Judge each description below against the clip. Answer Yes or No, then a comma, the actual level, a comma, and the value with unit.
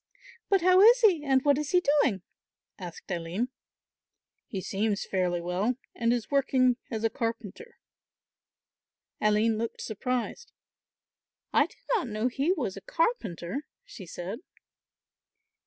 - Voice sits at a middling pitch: No, high, 235 Hz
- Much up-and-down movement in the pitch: Yes, wide, 7.1 semitones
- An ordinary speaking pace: No, slow, 130 wpm